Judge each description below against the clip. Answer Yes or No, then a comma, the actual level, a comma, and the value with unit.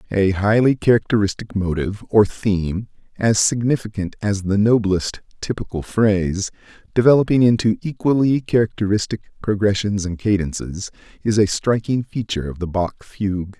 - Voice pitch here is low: Yes, low, 105 Hz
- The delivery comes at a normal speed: No, slow, 125 wpm